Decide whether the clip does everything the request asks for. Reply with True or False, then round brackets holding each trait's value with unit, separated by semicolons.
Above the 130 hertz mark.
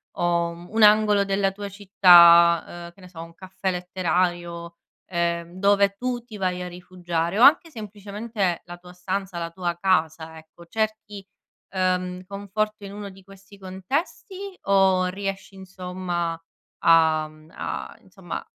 True (185 Hz)